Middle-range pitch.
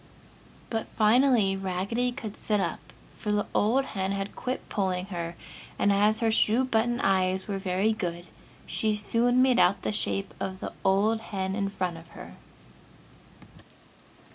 No: high, 205 Hz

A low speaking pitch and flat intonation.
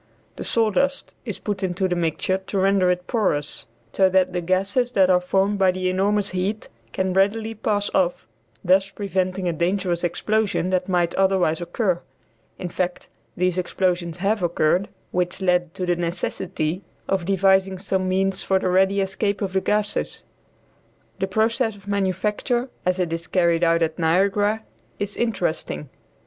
No: high, 190 Hz; narrow, 2.1 semitones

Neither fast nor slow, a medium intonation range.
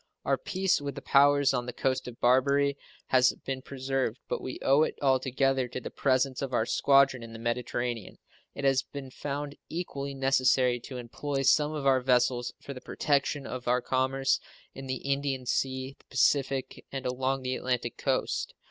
No: average, 180 wpm; narrow, 1.6 semitones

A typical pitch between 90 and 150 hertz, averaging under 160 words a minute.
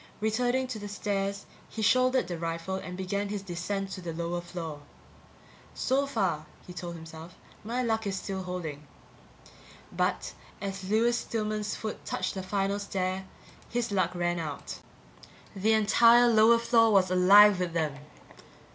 No: high, 195 Hz; average, 150 wpm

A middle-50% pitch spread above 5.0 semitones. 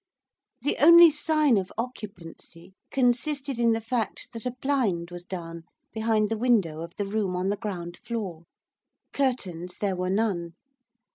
Yes: wide, 5.6 semitones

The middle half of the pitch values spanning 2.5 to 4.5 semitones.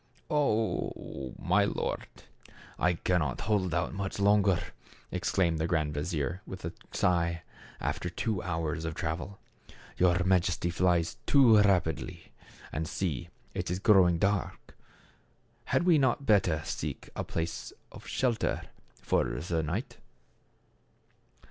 Yes: average, 3.4 semitones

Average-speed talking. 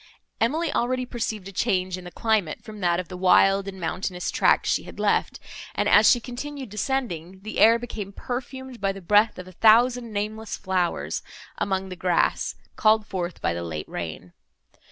Yes: average, 180 wpm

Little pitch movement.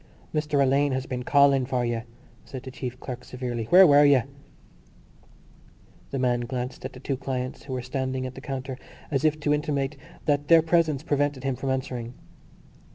Yes: narrow, 2.2 semitones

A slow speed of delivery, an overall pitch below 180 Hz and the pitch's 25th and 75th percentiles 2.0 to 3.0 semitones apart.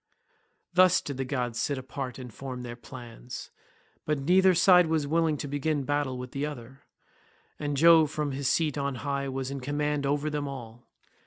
No: average, 180 wpm; medium, 140 Hz; narrow, 2.6 semitones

